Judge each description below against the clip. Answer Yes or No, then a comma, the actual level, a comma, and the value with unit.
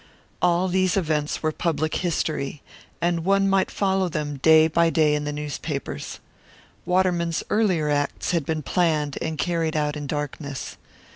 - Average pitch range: Yes, average, 3.0 semitones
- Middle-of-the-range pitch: Yes, medium, 160 Hz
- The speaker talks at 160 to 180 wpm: No, average, 150 wpm